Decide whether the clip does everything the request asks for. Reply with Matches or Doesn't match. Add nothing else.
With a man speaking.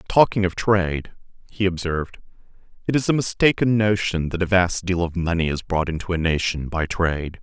Matches